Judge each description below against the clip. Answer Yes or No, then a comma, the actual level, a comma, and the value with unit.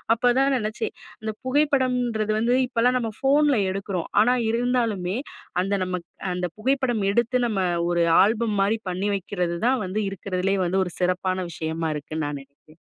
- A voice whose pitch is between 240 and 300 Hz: No, high, 210 Hz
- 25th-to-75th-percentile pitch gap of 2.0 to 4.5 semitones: No, average, 5.1 semitones